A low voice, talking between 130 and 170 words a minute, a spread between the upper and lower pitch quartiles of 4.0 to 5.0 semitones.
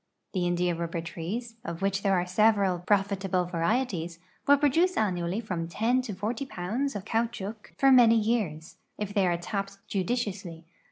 No: high, 195 Hz; average, 165 wpm; average, 4.4 semitones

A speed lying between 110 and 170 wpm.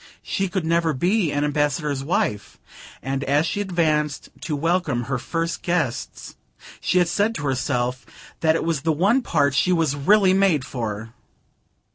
Yes: average, 155 wpm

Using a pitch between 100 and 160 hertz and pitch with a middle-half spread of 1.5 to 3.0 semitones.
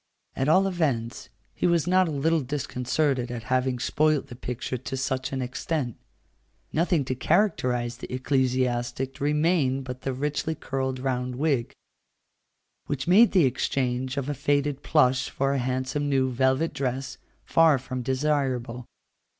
Yes: low, 135 Hz; average, 2.7 semitones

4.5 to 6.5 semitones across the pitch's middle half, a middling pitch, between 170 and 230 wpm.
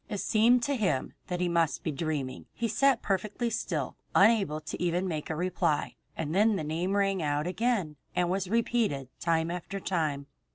Yes: average, 5.1 semitones; medium, 180 Hz; average, 190 wpm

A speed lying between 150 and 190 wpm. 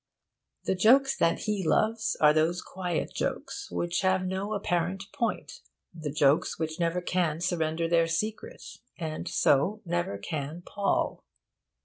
No: slow, 135 wpm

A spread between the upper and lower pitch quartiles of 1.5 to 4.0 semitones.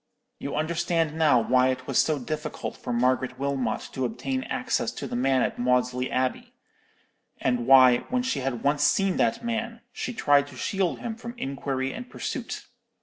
No: average, 4.6 semitones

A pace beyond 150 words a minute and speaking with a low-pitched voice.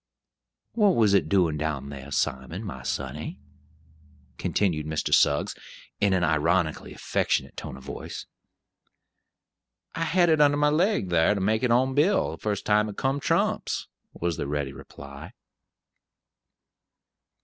No: average, 140 wpm; very low, 95 Hz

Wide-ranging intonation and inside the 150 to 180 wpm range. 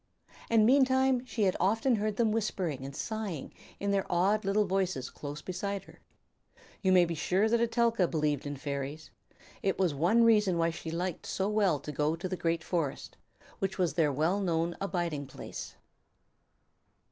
No: average, 4.8 semitones; average, 170 wpm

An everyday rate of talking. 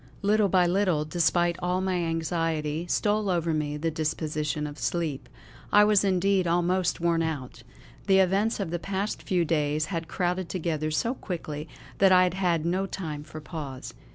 Yes: average, 170 wpm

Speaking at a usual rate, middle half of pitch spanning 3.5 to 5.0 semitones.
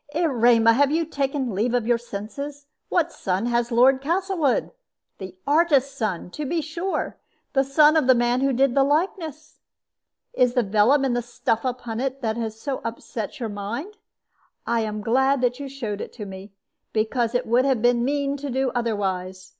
Yes: average, 185 wpm; average, 3.8 semitones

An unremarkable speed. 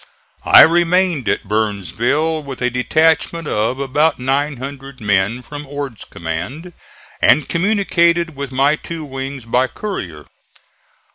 No: slow, 120 wpm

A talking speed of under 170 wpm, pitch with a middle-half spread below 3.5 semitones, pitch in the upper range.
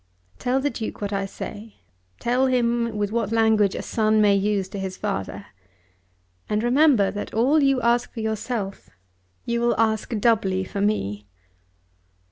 Yes: average, 155 wpm; average, 2.9 semitones; high, 220 Hz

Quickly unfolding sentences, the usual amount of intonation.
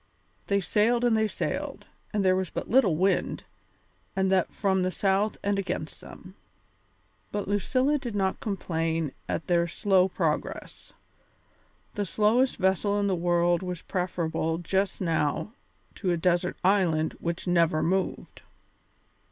No: average, 140 wpm; average, 3.0 semitones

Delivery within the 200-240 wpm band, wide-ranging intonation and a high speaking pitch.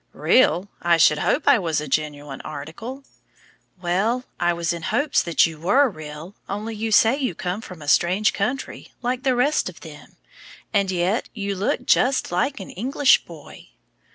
No: average, 175 wpm; wide, 6.6 semitones; high, 195 Hz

